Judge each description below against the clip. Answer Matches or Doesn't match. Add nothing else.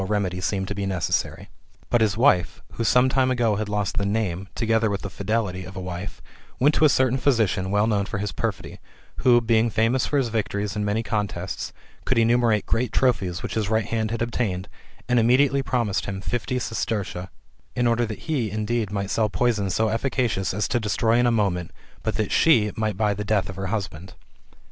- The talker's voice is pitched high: Doesn't match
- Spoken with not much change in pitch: Doesn't match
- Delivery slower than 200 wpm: Doesn't match